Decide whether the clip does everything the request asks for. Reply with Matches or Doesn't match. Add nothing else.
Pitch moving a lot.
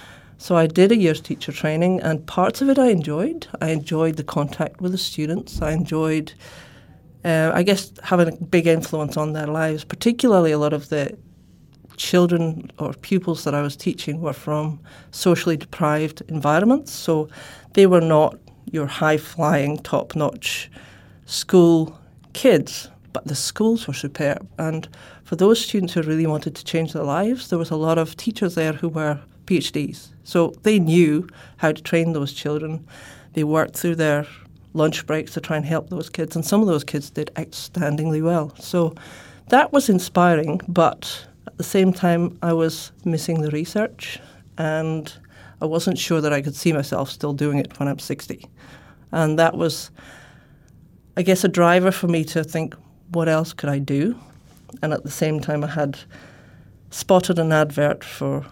Doesn't match